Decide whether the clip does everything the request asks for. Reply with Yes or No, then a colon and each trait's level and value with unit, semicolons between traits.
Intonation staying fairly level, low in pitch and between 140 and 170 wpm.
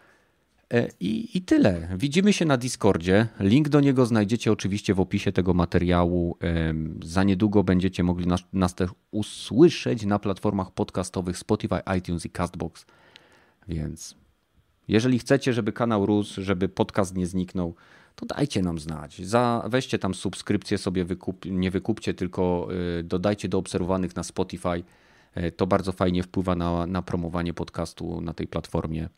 No: average, 3.1 semitones; very low, 95 Hz; average, 145 wpm